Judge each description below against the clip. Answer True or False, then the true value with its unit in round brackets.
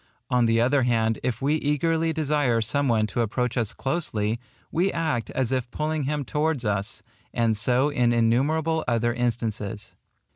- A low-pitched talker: True (125 Hz)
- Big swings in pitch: False (4.5 semitones)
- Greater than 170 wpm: False (160 wpm)